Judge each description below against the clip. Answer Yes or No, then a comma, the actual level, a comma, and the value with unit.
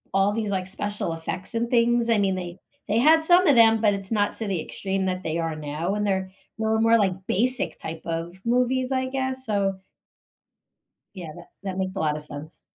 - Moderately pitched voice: No, high, 200 Hz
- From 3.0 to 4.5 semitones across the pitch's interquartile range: Yes, average, 4.1 semitones